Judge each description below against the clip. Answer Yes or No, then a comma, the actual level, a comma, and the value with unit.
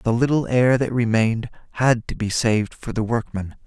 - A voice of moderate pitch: No, low, 115 Hz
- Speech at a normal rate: Yes, average, 195 wpm